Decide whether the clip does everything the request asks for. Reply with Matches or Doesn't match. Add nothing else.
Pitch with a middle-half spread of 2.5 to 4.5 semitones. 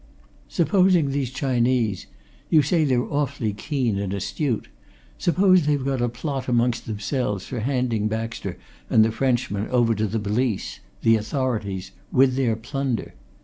Matches